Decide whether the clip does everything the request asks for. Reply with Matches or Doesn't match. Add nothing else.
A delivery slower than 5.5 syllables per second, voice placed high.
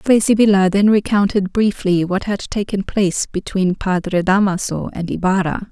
Matches